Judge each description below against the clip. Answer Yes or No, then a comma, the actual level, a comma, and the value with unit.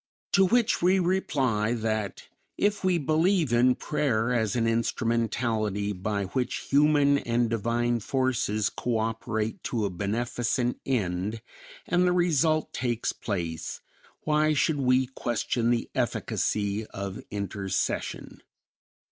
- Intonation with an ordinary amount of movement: Yes, average, 4.8 semitones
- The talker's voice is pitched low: Yes, low, 120 Hz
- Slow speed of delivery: Yes, slow, 115 wpm